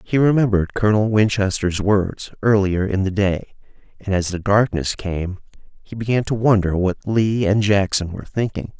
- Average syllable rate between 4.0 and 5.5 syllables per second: Yes, 5.0 syllables/s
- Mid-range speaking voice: No, low, 100 Hz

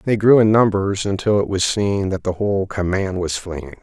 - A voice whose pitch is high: No, low, 100 Hz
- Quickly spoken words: Yes, fast, 220 wpm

